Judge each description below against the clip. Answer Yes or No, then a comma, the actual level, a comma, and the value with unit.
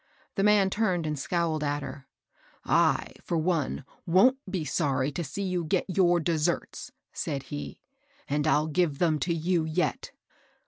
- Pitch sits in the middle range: Yes, medium, 165 Hz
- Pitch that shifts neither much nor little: Yes, average, 3.6 semitones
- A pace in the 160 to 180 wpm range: Yes, average, 170 wpm